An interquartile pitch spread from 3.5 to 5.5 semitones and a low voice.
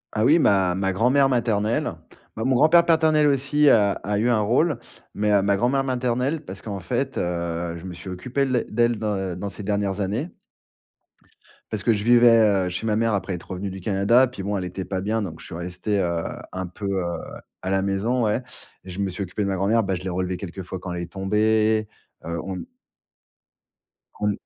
Yes: average, 4.1 semitones; low, 105 Hz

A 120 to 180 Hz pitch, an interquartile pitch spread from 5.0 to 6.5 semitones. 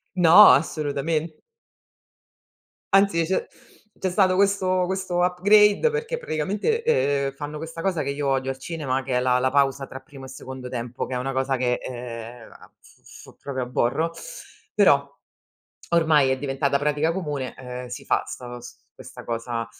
Yes: medium, 140 Hz; wide, 5.4 semitones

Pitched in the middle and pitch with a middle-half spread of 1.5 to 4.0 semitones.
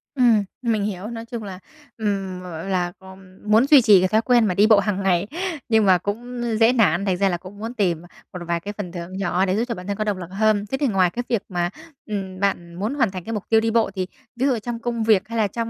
No: high, 205 Hz; average, 3.4 semitones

